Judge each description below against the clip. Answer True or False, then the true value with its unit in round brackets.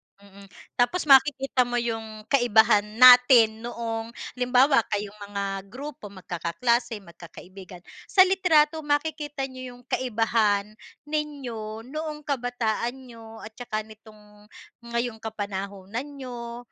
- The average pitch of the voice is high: True (235 Hz)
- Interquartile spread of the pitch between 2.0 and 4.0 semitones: True (3.7 semitones)